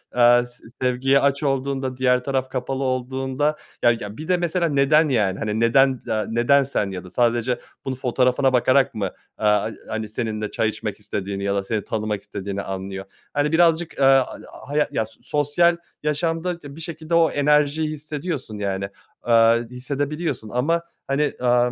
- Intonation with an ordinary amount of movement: Yes, average, 4.8 semitones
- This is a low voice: Yes, low, 130 Hz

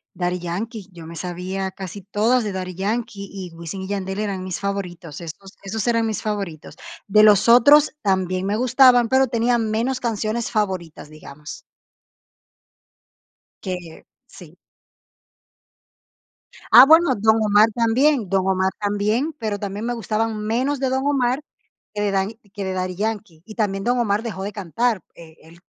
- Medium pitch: No, high, 205 Hz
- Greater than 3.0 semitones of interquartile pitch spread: Yes, average, 3.6 semitones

